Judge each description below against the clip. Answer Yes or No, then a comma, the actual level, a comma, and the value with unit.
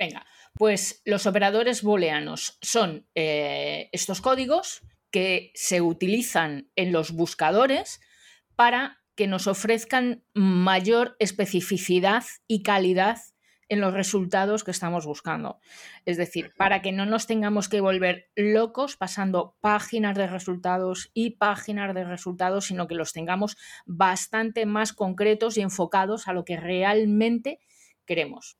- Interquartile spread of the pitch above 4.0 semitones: No, average, 3.1 semitones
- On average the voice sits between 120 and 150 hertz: No, high, 195 Hz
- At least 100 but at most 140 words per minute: Yes, average, 130 wpm